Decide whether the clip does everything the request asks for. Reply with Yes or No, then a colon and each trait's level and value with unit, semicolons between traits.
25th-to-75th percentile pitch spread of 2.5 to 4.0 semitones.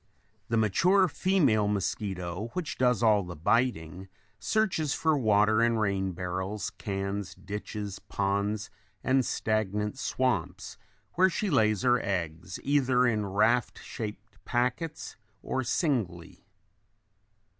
No: average, 4.5 semitones